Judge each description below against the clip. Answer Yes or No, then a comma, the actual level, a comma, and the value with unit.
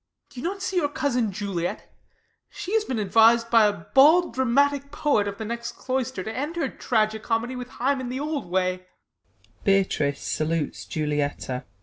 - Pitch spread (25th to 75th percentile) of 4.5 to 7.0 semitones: Yes, average, 4.8 semitones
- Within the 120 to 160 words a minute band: Yes, average, 150 wpm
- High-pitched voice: Yes, high, 245 Hz